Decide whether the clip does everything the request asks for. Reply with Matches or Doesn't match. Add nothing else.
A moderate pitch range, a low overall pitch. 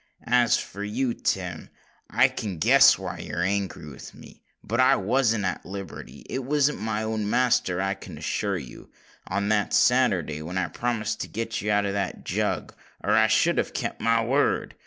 Matches